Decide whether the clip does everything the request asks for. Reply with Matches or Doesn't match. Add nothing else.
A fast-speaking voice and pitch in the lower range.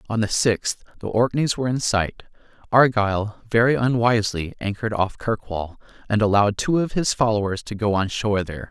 Doesn't match